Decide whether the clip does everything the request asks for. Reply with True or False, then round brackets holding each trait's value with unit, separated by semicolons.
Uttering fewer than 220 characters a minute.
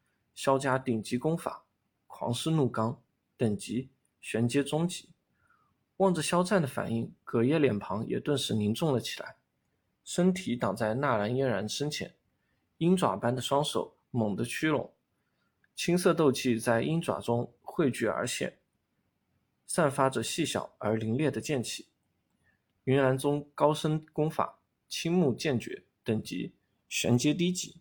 True (205 characters per minute)